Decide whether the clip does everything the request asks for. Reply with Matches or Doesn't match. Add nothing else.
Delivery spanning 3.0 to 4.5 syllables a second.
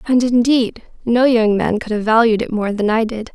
Doesn't match